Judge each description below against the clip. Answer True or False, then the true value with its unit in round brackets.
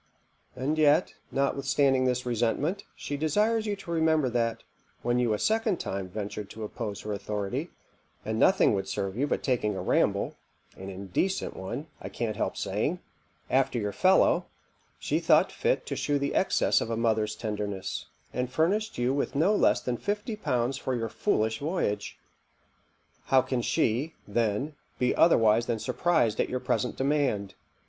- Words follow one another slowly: False (165 wpm)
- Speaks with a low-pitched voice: True (125 Hz)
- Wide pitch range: True (5.9 semitones)